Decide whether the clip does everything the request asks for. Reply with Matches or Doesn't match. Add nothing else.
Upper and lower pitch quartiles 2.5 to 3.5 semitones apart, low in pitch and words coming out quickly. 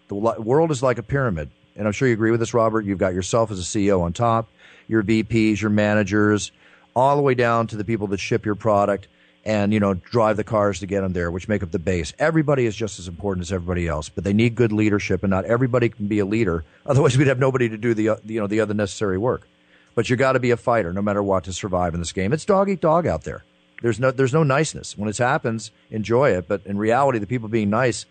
Matches